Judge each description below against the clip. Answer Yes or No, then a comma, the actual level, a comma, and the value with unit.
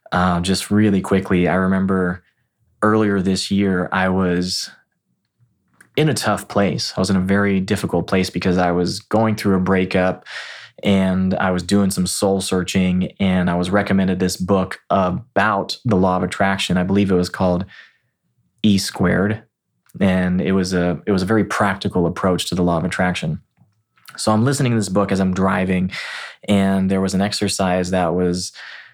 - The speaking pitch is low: Yes, very low, 95 Hz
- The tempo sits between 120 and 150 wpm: No, average, 175 wpm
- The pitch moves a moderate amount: No, narrow, 1.5 semitones